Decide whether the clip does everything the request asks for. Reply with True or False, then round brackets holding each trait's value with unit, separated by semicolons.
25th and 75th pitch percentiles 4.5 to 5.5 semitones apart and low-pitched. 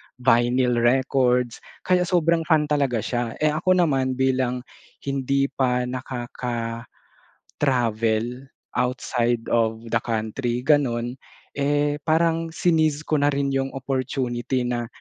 False (3.1 semitones; 130 Hz)